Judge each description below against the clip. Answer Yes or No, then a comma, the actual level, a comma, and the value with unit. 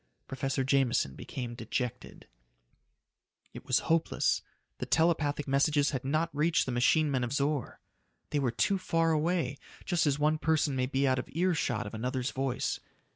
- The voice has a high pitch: No, medium, 140 Hz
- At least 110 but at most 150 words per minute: No, average, 160 wpm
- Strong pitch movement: No, average, 3.4 semitones